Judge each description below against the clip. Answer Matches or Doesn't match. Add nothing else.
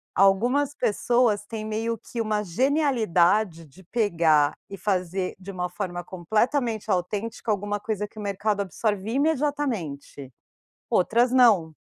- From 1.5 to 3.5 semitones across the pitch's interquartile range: Doesn't match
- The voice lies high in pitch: Matches